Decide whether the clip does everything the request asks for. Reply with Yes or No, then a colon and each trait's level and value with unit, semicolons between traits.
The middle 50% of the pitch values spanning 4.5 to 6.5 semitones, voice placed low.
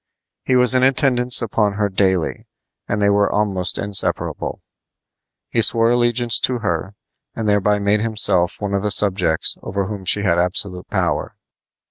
No: average, 3.0 semitones; low, 105 Hz